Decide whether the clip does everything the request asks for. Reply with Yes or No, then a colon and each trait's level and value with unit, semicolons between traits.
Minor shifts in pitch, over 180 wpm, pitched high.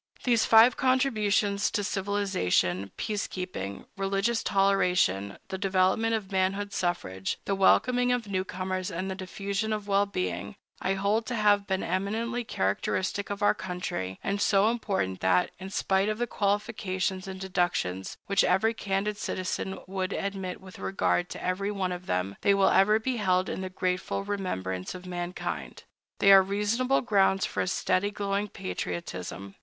No: narrow, 2.1 semitones; average, 150 wpm; high, 195 Hz